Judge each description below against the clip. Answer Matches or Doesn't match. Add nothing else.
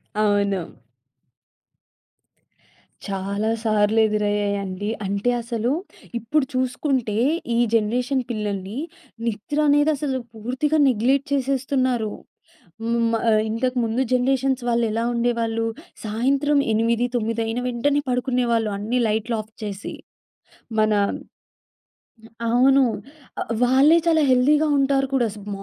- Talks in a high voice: Matches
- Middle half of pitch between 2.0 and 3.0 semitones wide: Doesn't match